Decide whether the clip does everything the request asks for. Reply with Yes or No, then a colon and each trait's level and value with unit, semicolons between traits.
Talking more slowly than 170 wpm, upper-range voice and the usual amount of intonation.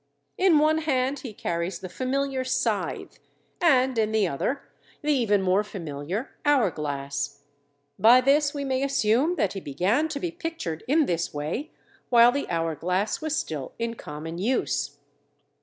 No: average, 155 wpm; high, 230 Hz; wide, 8.5 semitones